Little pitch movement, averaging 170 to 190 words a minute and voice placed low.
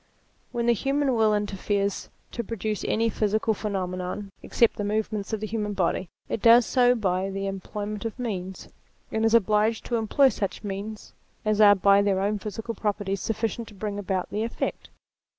No: narrow, 2.2 semitones; average, 175 wpm; high, 210 Hz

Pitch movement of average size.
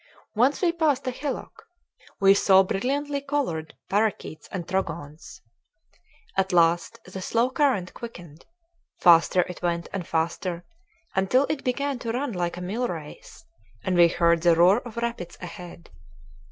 No: wide, 6.4 semitones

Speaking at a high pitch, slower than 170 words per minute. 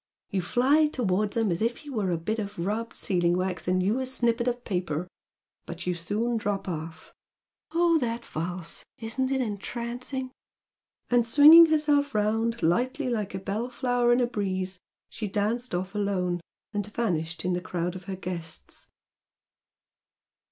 Yes: high, 210 Hz; average, 160 wpm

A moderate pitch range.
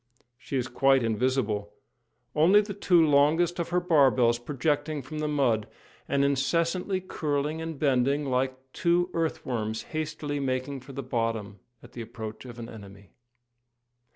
Yes: average, 4.6 semitones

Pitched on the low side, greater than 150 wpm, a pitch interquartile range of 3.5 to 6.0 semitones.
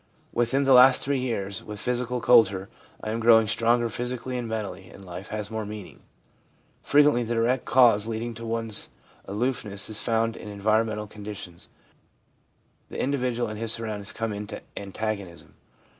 No: low, 110 Hz; average, 160 wpm; narrow, 2.6 semitones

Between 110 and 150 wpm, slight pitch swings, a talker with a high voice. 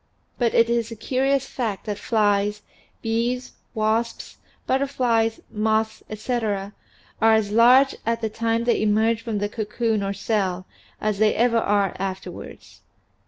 Yes: average, 140 wpm; narrow, 2.0 semitones; high, 225 Hz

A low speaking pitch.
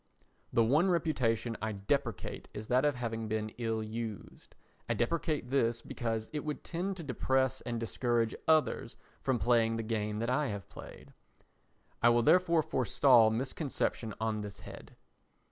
Yes: low, 120 Hz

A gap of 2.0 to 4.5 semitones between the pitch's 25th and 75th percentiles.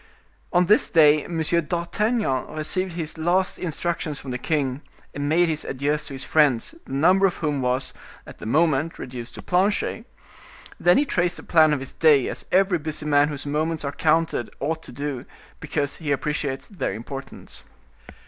Yes: average, 3.5 semitones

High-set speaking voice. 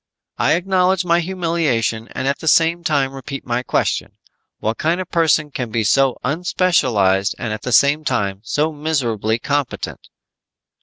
No: medium, 140 Hz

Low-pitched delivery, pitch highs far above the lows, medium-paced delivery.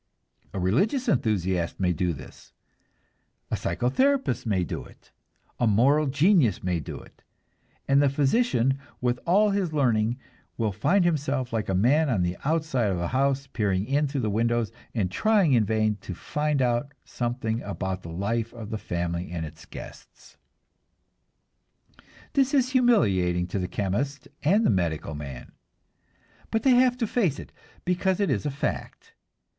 Yes: low, 120 Hz; wide, 8.0 semitones; average, 160 wpm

